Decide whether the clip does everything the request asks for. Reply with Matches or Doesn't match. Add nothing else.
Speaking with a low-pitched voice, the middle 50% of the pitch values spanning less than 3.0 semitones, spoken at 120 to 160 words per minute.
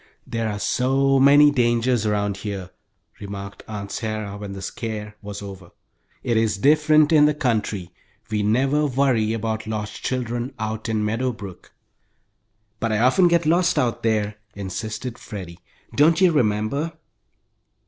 Doesn't match